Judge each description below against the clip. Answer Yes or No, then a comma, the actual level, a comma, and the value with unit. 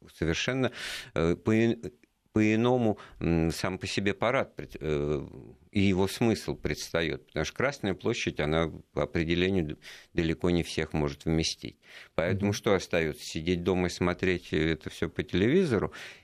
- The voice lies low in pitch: Yes, very low, 90 Hz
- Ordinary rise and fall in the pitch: Yes, average, 3.5 semitones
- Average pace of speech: Yes, average, 125 wpm